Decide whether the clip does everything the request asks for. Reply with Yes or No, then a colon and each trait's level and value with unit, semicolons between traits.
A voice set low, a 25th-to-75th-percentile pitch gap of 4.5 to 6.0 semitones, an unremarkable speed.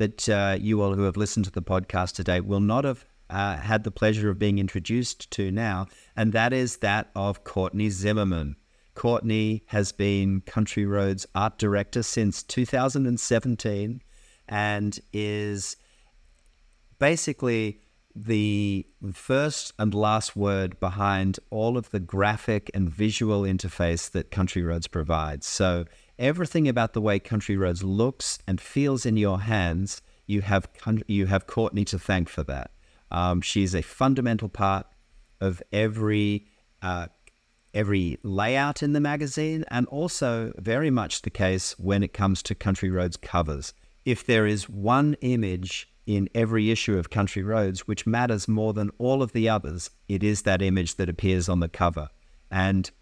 No: low, 105 Hz; average, 3.0 semitones; average, 155 wpm